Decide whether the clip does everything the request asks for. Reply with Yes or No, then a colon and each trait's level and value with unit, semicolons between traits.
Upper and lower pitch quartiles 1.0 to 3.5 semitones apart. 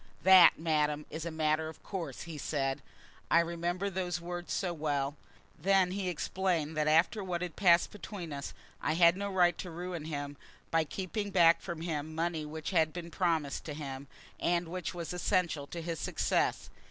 Yes: narrow, 2.5 semitones